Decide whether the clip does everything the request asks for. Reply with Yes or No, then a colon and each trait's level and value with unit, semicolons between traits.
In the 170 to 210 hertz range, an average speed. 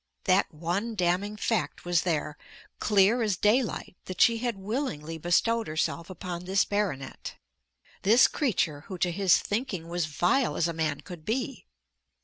Yes: medium, 185 Hz; average, 150 wpm